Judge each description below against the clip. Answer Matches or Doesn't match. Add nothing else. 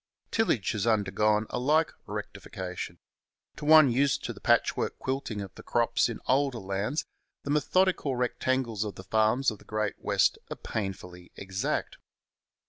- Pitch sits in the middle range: Doesn't match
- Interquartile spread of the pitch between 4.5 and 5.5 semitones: Matches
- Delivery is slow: Doesn't match